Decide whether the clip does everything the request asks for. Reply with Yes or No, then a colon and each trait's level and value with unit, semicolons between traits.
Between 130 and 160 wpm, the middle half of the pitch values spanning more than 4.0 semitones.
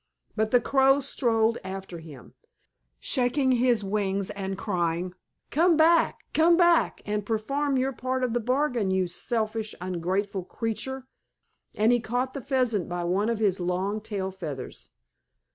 Yes: average, 145 wpm; average, 5.2 semitones